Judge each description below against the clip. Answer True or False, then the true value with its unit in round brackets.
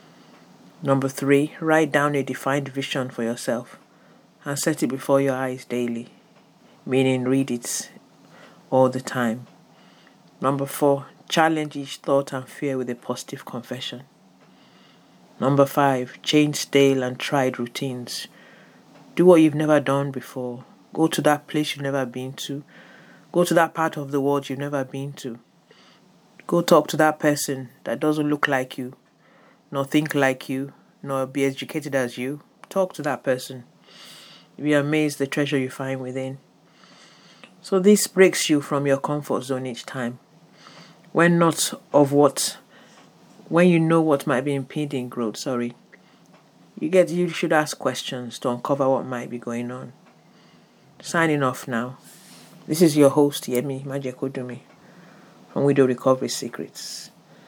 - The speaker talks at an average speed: True (150 wpm)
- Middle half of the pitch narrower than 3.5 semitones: True (2.7 semitones)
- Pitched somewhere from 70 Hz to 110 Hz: False (140 Hz)